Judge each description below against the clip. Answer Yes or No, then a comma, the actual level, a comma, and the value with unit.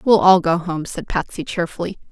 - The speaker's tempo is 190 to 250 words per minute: Yes, average, 200 wpm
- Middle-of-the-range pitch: Yes, medium, 180 Hz